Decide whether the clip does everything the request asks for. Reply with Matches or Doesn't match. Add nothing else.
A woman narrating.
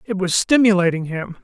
Doesn't match